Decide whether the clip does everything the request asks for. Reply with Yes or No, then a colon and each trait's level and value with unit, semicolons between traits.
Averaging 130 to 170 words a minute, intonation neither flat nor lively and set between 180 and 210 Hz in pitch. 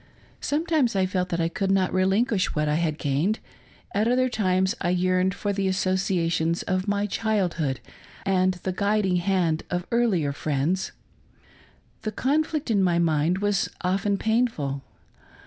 Yes: average, 145 wpm; average, 3.2 semitones; medium, 185 Hz